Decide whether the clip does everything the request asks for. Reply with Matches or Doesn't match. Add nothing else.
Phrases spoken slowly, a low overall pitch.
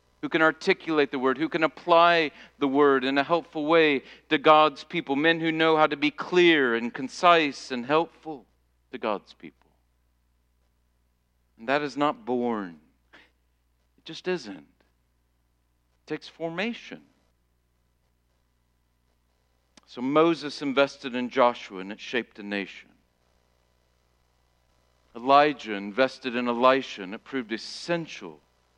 Matches